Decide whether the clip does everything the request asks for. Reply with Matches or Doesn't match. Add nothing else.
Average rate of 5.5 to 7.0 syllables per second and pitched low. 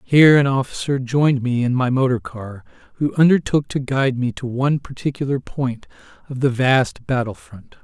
Doesn't match